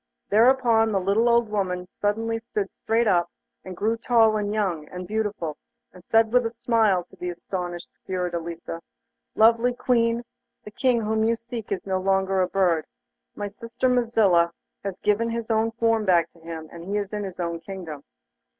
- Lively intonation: No, average, 4.0 semitones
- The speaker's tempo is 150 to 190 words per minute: Yes, average, 175 wpm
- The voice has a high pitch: Yes, high, 210 Hz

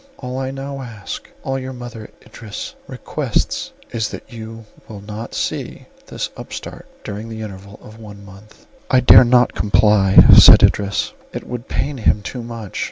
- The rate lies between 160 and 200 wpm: Yes, average, 165 wpm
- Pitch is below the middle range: Yes, low, 110 Hz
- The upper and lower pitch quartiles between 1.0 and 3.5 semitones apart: Yes, average, 3.1 semitones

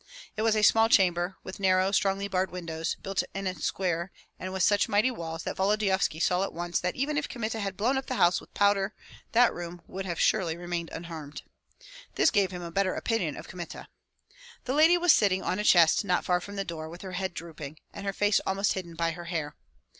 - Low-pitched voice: No, high, 190 Hz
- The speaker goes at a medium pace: No, fast, 220 wpm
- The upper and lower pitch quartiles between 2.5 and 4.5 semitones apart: Yes, average, 2.9 semitones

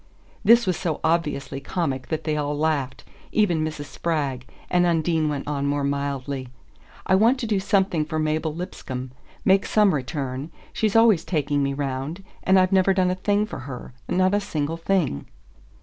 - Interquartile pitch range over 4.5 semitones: Yes, average, 4.9 semitones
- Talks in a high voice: No, medium, 155 Hz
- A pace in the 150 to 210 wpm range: Yes, average, 175 wpm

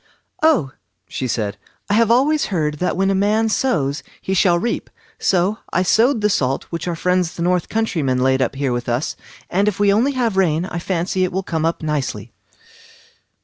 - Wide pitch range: Yes, wide, 5.7 semitones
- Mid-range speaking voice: Yes, medium, 180 Hz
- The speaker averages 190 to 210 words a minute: Yes, average, 200 wpm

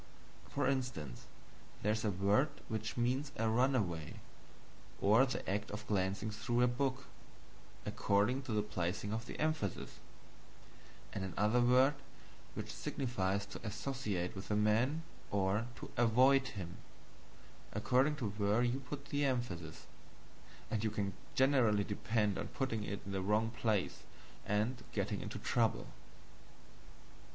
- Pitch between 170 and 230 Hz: No, low, 110 Hz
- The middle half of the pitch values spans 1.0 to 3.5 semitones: No, average, 3.9 semitones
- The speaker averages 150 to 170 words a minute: No, slow, 135 wpm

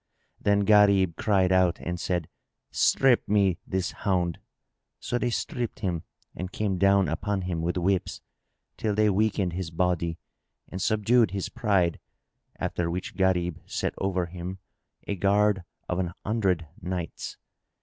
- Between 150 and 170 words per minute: No, average, 140 wpm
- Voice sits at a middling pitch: No, very low, 95 Hz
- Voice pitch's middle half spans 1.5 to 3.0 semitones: Yes, narrow, 2.6 semitones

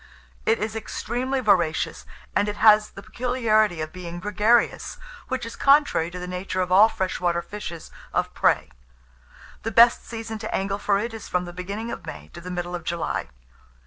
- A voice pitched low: No, high, 205 Hz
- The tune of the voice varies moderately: Yes, average, 4.0 semitones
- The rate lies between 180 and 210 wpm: Yes, average, 185 wpm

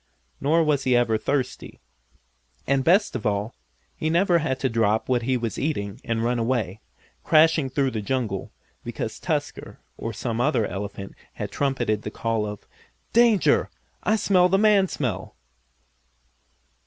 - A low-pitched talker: Yes, low, 130 Hz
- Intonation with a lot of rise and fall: Yes, wide, 6.0 semitones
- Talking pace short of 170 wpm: Yes, average, 150 wpm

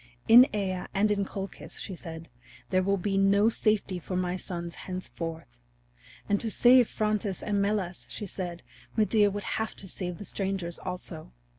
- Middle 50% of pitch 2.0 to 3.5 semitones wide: Yes, narrow, 2.5 semitones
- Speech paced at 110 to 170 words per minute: Yes, average, 165 wpm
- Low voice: No, high, 195 Hz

